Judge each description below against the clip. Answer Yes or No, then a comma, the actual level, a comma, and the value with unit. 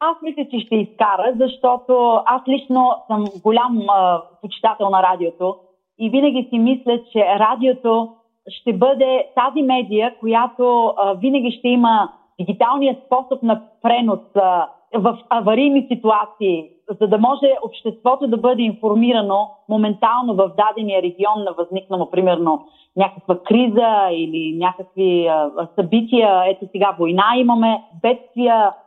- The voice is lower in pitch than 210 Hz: No, high, 220 Hz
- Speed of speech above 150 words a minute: No, average, 125 wpm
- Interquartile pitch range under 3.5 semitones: No, average, 4.1 semitones